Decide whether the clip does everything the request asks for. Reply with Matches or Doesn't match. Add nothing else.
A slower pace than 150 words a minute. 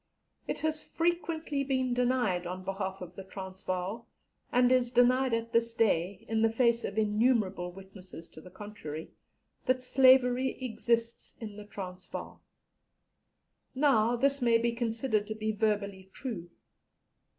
Matches